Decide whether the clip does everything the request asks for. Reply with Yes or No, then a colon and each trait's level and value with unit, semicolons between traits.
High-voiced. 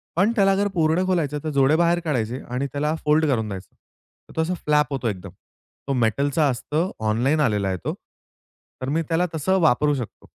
No: medium, 150 Hz